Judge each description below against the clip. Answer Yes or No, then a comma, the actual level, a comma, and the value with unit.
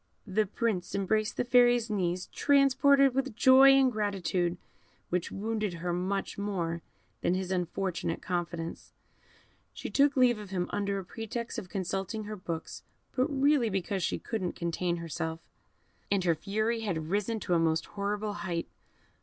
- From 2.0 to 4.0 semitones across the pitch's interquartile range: No, average, 4.4 semitones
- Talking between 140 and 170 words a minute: Yes, average, 155 wpm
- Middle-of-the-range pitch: No, high, 200 Hz